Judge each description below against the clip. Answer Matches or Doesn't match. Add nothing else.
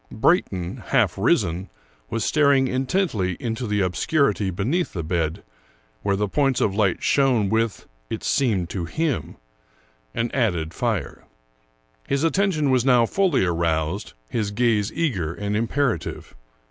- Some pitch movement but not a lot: Doesn't match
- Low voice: Matches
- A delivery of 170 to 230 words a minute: Doesn't match